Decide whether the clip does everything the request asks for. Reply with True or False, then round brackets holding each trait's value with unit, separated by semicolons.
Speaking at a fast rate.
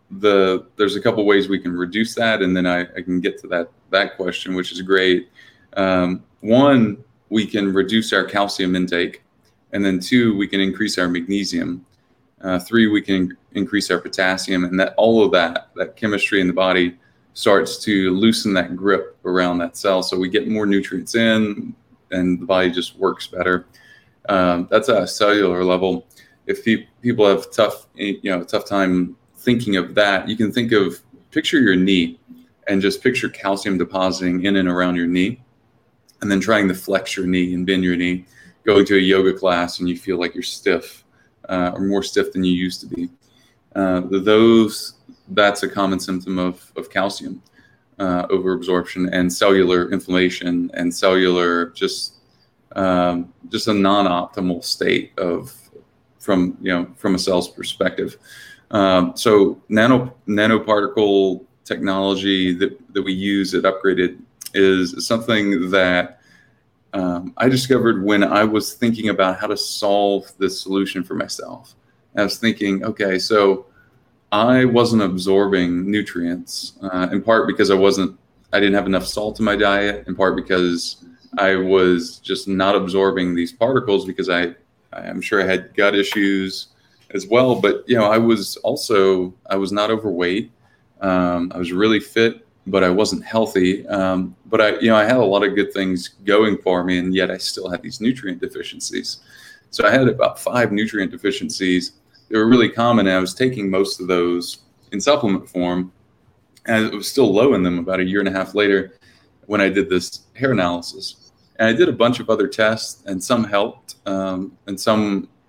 False (175 wpm)